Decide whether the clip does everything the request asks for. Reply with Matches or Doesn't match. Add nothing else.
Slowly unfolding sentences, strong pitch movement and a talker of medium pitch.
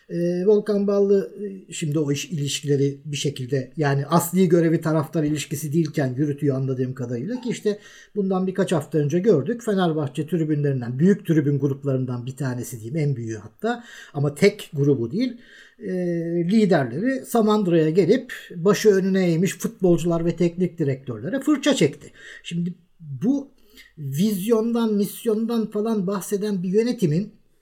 Doesn't match